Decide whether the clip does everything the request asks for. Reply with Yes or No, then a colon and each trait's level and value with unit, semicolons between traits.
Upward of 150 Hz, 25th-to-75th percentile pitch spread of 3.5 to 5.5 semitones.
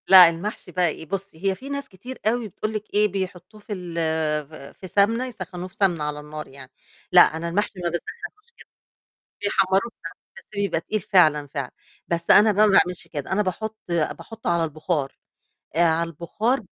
Yes: medium, 185 Hz; average, 4.0 semitones